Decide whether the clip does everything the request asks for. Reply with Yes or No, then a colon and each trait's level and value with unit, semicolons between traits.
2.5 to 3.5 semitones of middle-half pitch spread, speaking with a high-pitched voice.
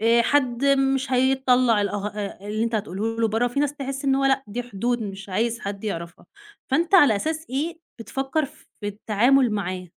No: average, 4.6 semitones; high, 240 Hz